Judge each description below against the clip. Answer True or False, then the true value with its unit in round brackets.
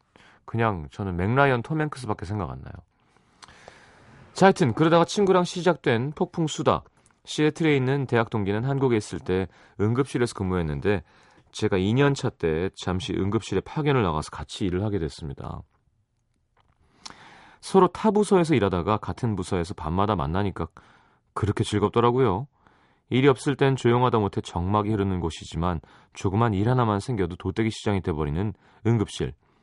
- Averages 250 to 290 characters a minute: False (340 characters per minute)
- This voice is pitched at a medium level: False (110 Hz)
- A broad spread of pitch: True (5.9 semitones)